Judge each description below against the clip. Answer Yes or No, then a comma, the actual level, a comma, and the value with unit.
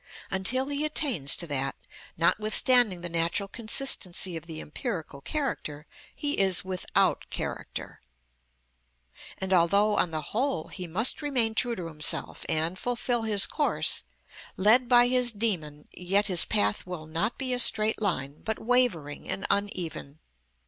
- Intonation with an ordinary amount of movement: No, wide, 6.6 semitones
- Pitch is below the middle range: No, high, 195 Hz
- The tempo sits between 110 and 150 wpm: Yes, average, 140 wpm